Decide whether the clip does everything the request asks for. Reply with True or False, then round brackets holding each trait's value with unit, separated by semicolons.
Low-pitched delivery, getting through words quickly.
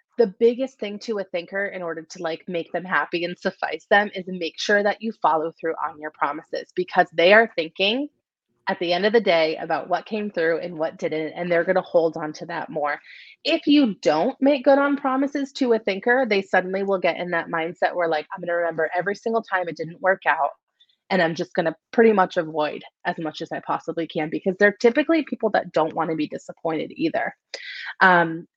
False (185 Hz; 220 wpm)